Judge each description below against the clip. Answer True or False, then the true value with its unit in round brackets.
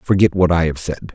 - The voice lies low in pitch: True (85 Hz)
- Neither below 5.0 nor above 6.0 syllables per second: True (5.4 syllables/s)